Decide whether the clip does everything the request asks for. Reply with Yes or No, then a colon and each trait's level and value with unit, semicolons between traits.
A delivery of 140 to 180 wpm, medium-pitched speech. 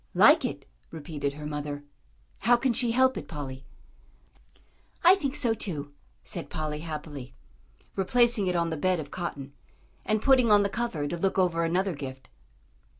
Yes: average, 160 wpm; medium, 170 Hz